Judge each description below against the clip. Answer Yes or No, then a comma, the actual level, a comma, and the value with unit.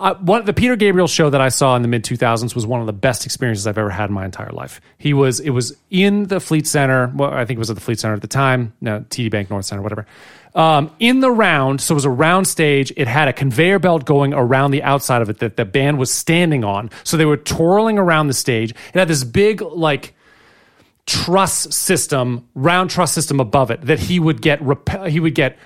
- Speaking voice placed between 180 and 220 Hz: No, medium, 140 Hz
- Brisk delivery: Yes, fast, 255 wpm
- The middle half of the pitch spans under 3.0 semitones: No, average, 5.1 semitones